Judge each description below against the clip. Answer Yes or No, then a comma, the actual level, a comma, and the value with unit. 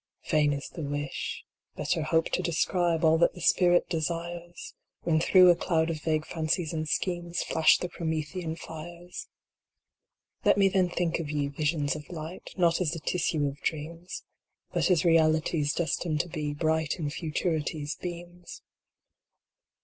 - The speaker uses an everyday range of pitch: No, narrow, 2.1 semitones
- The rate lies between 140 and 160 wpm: Yes, average, 155 wpm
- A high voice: No, medium, 165 Hz